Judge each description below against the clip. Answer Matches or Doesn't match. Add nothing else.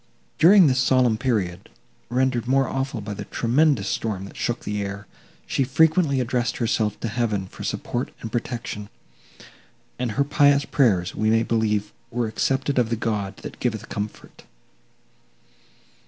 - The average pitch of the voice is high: Doesn't match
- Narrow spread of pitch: Doesn't match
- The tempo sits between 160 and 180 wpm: Doesn't match